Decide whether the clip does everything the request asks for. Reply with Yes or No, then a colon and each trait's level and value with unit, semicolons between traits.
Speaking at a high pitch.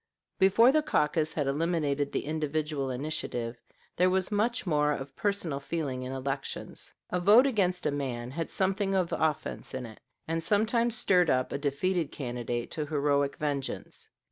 No: medium, 155 Hz